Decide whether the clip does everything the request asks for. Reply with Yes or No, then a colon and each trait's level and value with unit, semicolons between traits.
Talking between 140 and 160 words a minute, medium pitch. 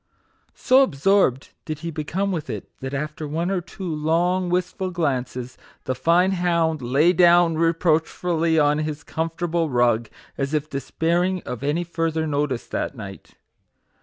Yes: average, 150 wpm; medium, 160 Hz